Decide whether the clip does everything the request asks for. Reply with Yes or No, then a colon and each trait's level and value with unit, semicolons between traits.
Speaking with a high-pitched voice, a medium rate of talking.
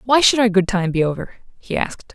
No: high, 205 Hz; fast, 250 wpm